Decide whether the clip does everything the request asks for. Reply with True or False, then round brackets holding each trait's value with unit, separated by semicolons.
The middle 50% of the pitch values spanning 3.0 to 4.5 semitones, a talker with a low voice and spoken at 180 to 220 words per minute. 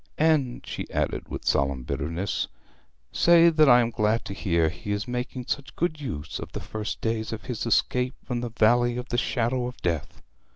True (3.5 semitones; 120 Hz; 195 wpm)